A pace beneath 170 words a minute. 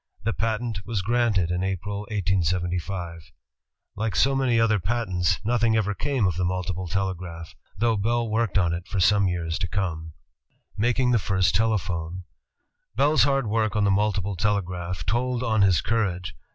Yes: average, 160 wpm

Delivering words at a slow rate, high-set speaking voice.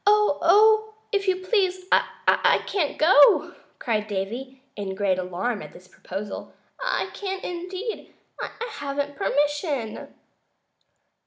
Yes: slow, 110 wpm; very high, 290 Hz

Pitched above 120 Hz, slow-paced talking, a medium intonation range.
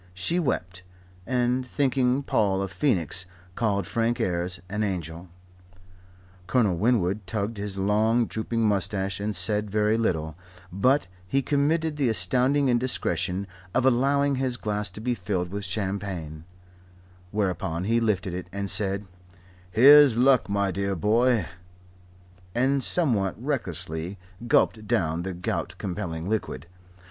No: low, 105 Hz; slow, 130 wpm; average, 5.0 semitones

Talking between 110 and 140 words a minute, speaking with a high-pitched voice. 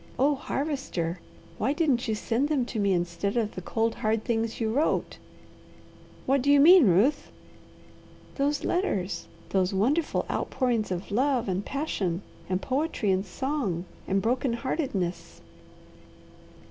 Yes: slow, 135 wpm; high, 230 Hz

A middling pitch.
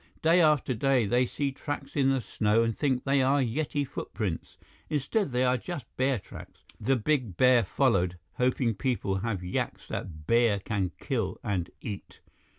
No: low, 125 Hz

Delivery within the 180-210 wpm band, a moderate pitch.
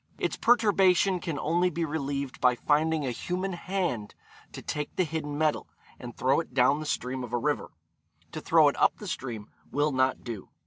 Yes: average, 190 wpm; medium, 150 Hz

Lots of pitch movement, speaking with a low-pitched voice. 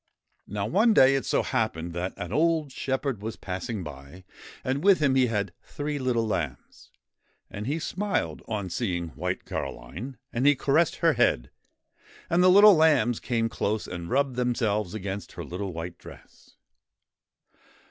Yes: wide, 7.3 semitones; low, 115 Hz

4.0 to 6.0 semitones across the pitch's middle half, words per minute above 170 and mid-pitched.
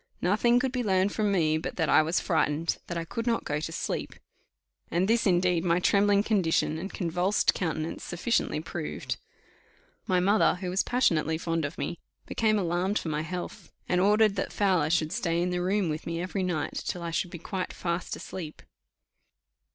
No: average, 3.3 semitones; average, 190 wpm; medium, 180 Hz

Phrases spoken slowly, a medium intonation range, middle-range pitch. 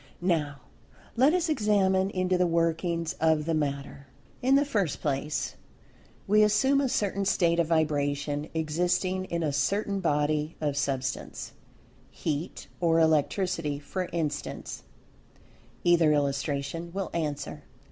Yes: slow, 120 wpm; average, 4.2 semitones; medium, 165 Hz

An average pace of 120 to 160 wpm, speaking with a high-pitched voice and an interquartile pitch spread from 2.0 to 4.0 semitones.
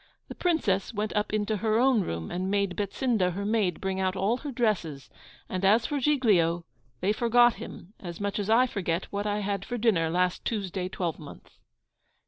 No: average, 190 wpm; high, 200 Hz; average, 3.7 semitones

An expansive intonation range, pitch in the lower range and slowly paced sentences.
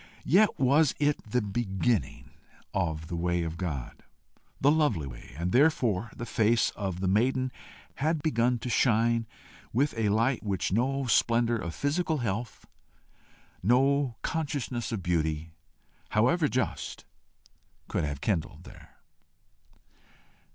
Yes: wide, 6.0 semitones; low, 115 Hz; slow, 125 wpm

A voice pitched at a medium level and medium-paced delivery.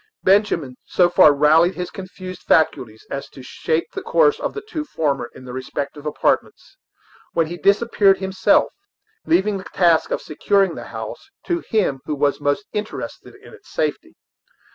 Yes: medium, 175 Hz; average, 165 wpm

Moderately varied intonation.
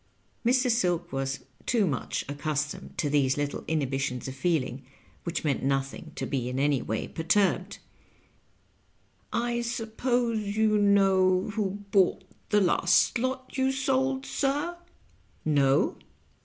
No: wide, 8.6 semitones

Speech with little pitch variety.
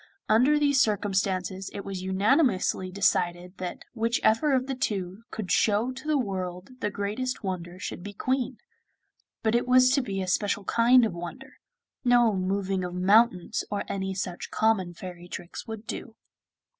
No: average, 4.4 semitones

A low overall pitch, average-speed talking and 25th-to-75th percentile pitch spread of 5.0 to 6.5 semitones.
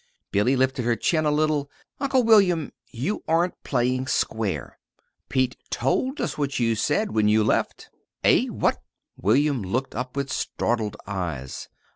Yes: low, 130 Hz; average, 145 wpm; wide, 5.5 semitones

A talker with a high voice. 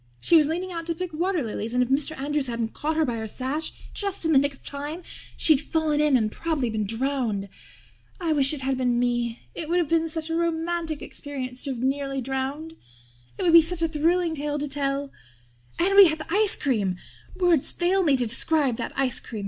Yes: very high, 295 Hz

